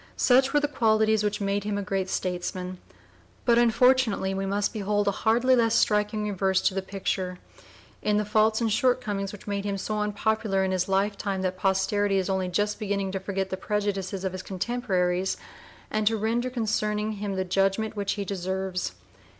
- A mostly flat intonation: Yes, narrow, 2.1 semitones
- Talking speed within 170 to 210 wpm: Yes, average, 185 wpm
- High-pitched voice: Yes, high, 205 Hz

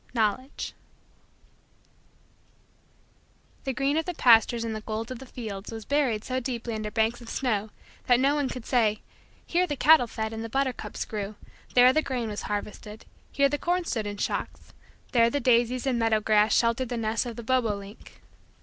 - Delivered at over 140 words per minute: Yes, average, 185 wpm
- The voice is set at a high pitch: Yes, high, 235 Hz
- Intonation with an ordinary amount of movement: Yes, average, 3.1 semitones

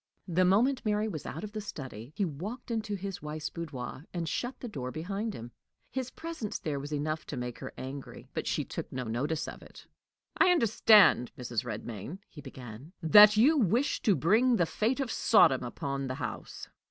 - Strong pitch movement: Yes, wide, 8.2 semitones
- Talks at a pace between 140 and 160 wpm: No, average, 190 wpm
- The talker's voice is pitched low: No, medium, 170 Hz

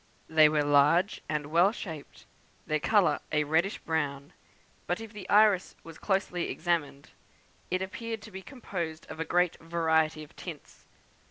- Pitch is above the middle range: No, medium, 165 Hz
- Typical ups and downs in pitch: Yes, average, 3.7 semitones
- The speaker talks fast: No, average, 155 wpm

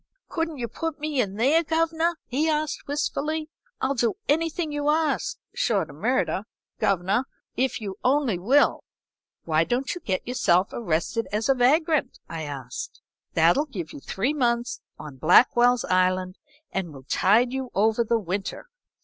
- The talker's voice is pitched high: Yes, high, 245 Hz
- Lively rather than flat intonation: Yes, wide, 7.7 semitones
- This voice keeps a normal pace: Yes, average, 155 wpm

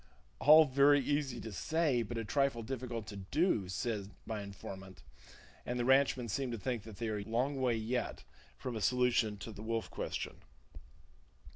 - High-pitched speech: No, low, 120 Hz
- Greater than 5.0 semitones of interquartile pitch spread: No, average, 3.7 semitones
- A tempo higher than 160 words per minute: Yes, average, 170 wpm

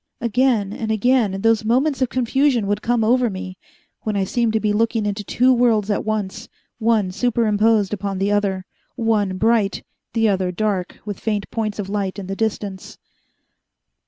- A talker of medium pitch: No, high, 215 Hz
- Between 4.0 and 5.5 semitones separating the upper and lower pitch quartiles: No, narrow, 2.5 semitones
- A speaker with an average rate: Yes, average, 170 wpm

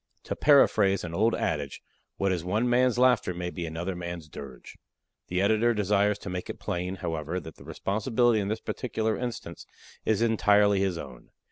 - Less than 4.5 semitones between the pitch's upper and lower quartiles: Yes, average, 4.1 semitones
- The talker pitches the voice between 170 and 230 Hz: No, low, 100 Hz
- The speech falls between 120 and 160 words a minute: No, average, 175 wpm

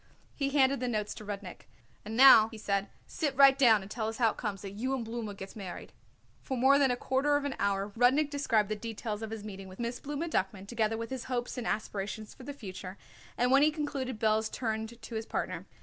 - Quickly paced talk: Yes, fast, 235 wpm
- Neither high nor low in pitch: No, high, 225 Hz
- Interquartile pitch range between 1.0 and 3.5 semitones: No, average, 4.0 semitones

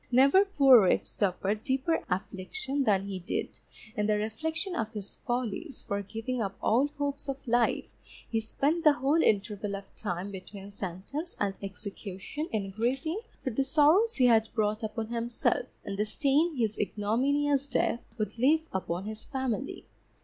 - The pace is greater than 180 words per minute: No, average, 160 wpm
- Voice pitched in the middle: No, high, 230 Hz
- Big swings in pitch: Yes, wide, 5.7 semitones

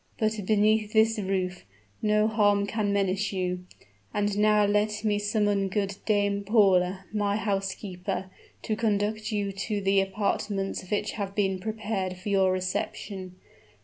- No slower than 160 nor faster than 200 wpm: No, average, 140 wpm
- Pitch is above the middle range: Yes, high, 205 Hz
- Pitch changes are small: Yes, narrow, 1.6 semitones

